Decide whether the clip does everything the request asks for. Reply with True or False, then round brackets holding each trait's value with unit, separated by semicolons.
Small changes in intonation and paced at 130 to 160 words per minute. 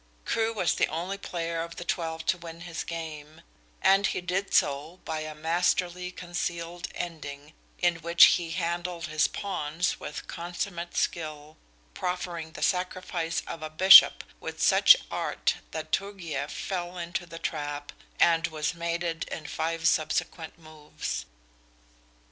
True (2.0 semitones; 140 wpm)